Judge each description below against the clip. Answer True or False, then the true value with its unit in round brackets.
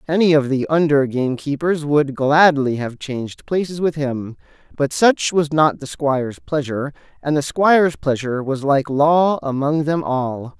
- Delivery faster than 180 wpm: False (165 wpm)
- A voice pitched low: False (145 Hz)